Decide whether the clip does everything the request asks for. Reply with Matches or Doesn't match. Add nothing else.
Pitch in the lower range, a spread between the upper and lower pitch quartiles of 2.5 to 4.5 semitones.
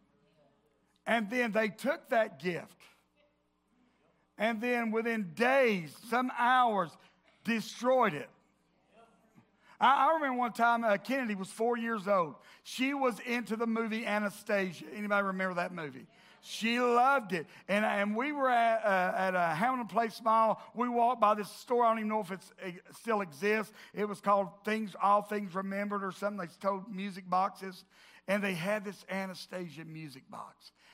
Doesn't match